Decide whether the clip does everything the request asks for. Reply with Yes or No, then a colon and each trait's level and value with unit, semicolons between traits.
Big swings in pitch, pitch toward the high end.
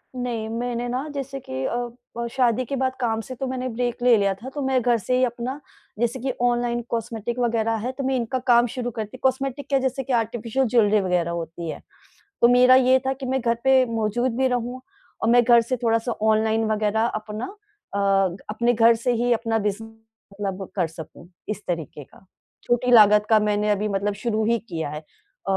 No: average, 2.9 semitones; high, 235 Hz